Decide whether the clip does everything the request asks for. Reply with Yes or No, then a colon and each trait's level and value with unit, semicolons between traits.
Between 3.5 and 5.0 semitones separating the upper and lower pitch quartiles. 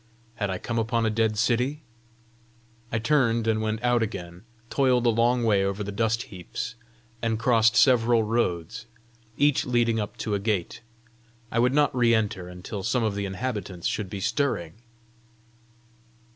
No: average, 2.8 semitones